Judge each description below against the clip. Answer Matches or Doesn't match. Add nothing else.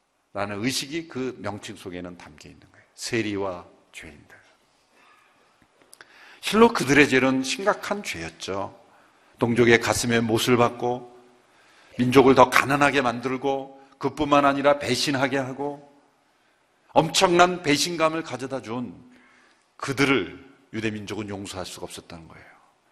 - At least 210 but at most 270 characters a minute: Matches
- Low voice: Matches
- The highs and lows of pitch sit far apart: Doesn't match